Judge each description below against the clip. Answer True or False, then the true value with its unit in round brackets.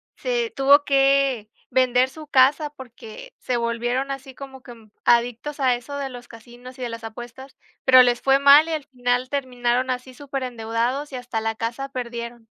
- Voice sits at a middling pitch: False (255 Hz)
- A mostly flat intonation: True (2.2 semitones)